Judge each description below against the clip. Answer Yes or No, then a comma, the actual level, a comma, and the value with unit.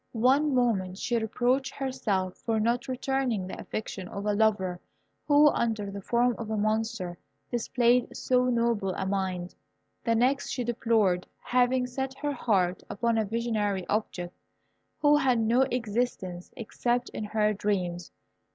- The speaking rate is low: No, average, 145 wpm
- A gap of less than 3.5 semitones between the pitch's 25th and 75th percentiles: No, average, 3.8 semitones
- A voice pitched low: No, high, 225 Hz